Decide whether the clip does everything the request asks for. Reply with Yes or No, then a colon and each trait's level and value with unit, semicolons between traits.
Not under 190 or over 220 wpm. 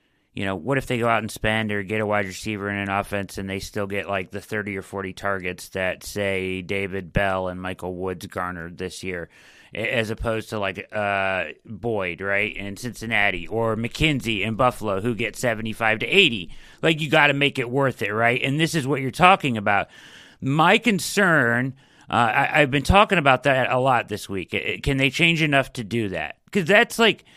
Yes: fast, 205 wpm